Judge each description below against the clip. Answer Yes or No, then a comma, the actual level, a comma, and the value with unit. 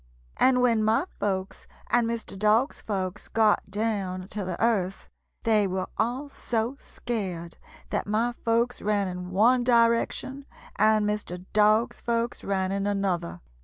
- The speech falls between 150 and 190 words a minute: No, average, 140 wpm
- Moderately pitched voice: No, high, 215 Hz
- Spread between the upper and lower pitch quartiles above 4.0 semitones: No, average, 3.3 semitones